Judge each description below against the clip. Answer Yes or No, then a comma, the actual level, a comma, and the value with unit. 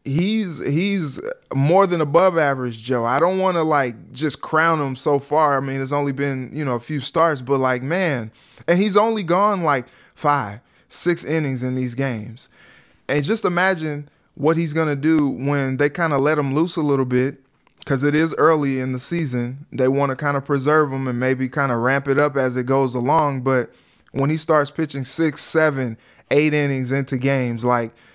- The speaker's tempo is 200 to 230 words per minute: Yes, fast, 205 wpm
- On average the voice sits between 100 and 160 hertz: Yes, medium, 140 Hz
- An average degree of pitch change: Yes, average, 3.4 semitones